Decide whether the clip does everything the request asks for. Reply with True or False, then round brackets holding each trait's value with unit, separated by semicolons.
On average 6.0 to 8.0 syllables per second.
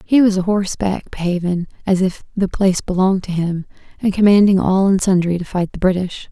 False (5.7 syllables/s)